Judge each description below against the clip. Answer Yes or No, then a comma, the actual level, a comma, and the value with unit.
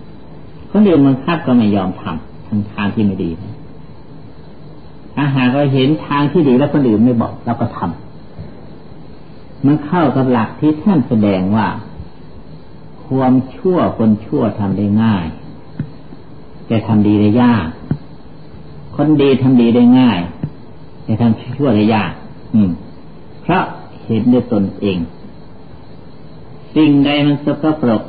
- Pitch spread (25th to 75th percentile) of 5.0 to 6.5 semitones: Yes, wide, 5.5 semitones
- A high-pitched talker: No, low, 120 Hz